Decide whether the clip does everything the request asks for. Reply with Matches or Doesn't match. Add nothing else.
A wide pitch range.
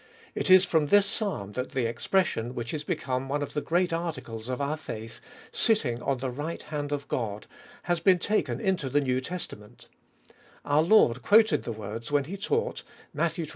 Matches